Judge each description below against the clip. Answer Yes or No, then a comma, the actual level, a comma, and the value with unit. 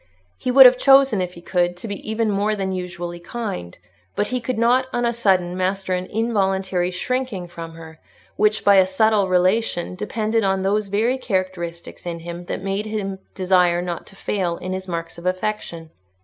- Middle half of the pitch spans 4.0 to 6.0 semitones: No, average, 3.4 semitones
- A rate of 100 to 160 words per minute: No, average, 190 wpm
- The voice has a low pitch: No, high, 190 Hz